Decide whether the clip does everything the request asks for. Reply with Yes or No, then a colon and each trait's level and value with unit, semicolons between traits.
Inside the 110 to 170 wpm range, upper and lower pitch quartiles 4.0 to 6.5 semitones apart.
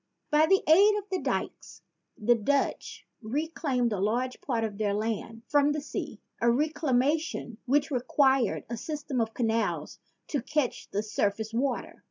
Yes: average, 160 wpm; average, 4.8 semitones